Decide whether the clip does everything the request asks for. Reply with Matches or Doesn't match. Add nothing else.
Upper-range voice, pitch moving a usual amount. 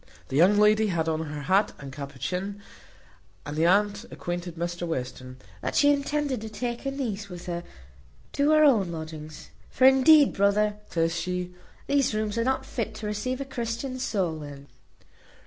Doesn't match